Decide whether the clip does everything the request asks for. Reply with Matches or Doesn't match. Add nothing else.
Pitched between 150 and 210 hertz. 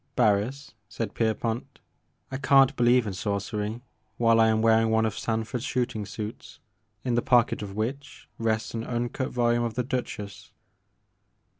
Doesn't match